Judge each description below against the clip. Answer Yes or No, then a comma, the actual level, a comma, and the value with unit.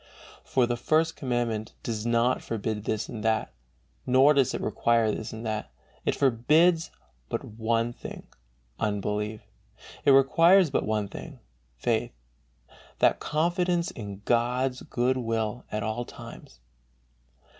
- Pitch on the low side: Yes, low, 120 Hz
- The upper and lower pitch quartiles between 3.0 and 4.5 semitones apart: Yes, average, 3.7 semitones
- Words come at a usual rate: No, slow, 130 wpm